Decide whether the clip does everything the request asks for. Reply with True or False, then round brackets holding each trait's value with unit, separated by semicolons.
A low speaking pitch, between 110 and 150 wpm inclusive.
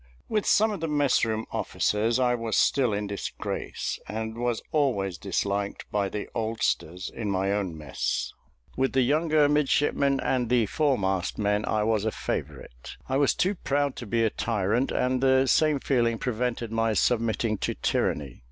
False (115 Hz; 170 wpm)